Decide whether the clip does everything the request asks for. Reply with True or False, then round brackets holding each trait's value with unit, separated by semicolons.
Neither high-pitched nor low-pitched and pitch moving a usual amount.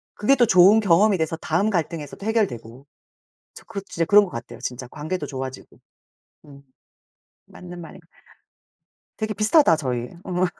False (175 Hz; 6.0 semitones)